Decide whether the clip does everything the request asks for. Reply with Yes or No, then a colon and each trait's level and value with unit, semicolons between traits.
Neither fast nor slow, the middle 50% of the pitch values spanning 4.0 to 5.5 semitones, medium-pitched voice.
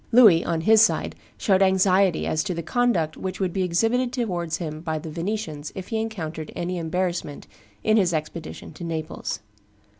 Yes: average, 175 wpm; average, 4.4 semitones; medium, 180 Hz